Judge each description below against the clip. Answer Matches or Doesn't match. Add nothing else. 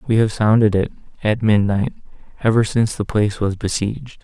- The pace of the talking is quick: Doesn't match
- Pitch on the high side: Doesn't match